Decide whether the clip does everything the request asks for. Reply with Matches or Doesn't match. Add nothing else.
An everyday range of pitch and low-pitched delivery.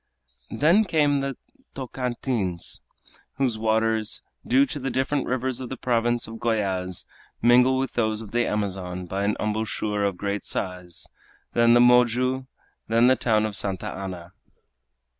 Matches